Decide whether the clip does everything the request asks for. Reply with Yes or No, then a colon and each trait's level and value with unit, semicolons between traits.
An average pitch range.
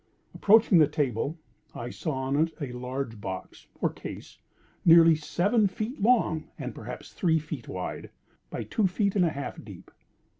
No: wide, 6.2 semitones